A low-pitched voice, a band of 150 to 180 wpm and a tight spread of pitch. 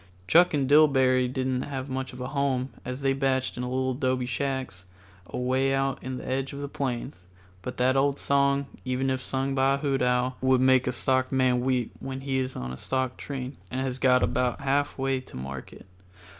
No: low, 130 Hz; average, 200 wpm; narrow, 1.1 semitones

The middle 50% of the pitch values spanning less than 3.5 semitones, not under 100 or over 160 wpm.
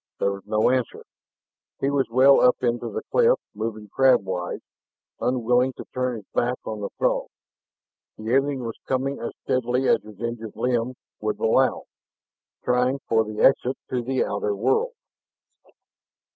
Yes: average, 3.0 semitones; average, 150 wpm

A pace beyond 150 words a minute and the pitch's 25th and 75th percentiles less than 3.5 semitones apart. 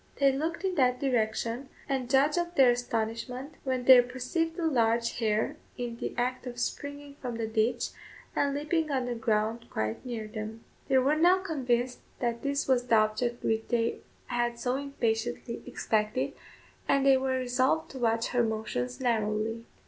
Yes: average, 170 wpm; average, 3.1 semitones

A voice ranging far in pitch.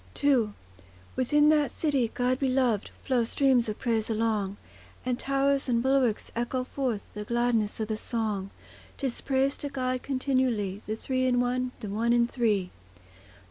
No: average, 3.2 semitones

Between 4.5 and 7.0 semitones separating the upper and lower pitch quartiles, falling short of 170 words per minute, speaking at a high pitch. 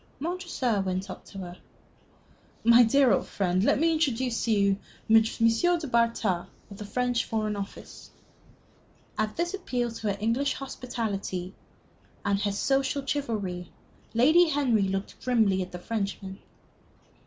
Yes: average, 4.9 semitones; average, 140 wpm; high, 225 Hz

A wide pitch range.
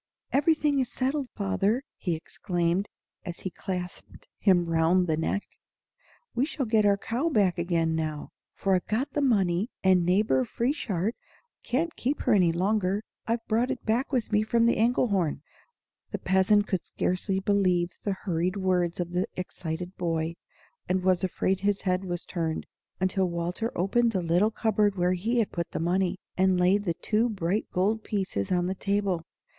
No: average, 3.7 semitones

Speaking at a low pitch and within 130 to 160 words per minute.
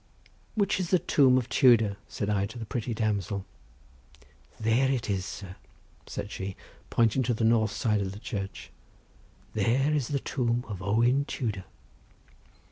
Yes: low, 115 Hz; average, 155 wpm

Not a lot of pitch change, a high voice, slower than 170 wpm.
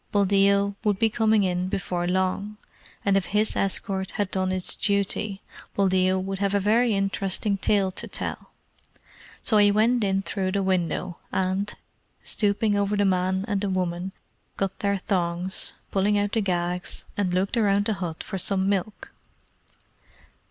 Yes: narrow, 1.5 semitones; high, 195 Hz; average, 160 wpm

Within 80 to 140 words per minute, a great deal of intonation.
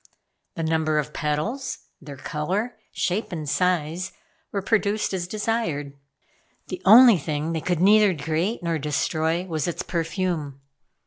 No: slow, 135 wpm; average, 4.3 semitones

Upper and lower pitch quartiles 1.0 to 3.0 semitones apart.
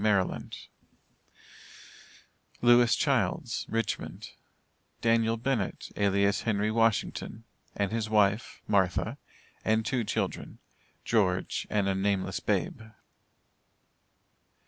Yes: narrow, 2.4 semitones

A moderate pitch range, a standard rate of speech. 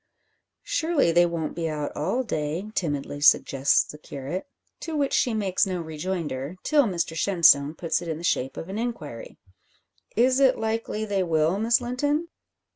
No: wide, 7.1 semitones; average, 165 wpm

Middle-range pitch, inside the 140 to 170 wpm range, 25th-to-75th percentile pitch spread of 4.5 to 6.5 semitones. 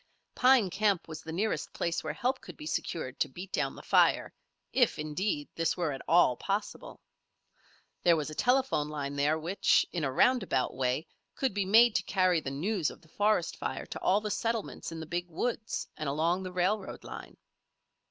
No: medium, 175 Hz; average, 190 wpm; average, 5.2 semitones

